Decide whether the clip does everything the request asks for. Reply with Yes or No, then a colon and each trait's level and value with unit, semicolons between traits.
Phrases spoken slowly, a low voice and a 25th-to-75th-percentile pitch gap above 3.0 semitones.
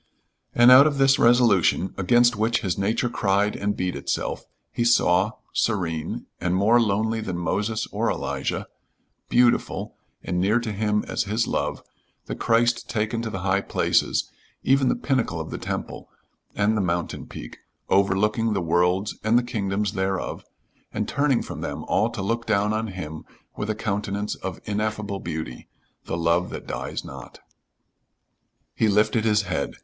No: average, 160 wpm; low, 105 Hz; average, 3.4 semitones